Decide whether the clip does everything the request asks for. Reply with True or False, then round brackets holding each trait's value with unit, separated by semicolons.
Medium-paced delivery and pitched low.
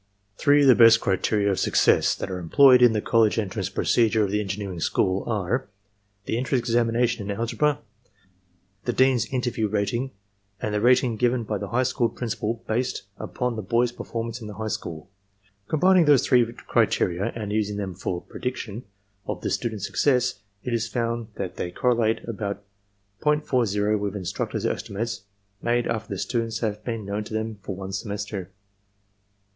True (170 wpm; 110 Hz)